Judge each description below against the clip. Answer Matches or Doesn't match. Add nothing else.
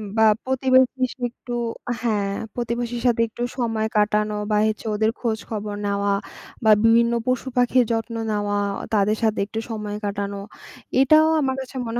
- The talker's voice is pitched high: Matches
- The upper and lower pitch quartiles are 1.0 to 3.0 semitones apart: Matches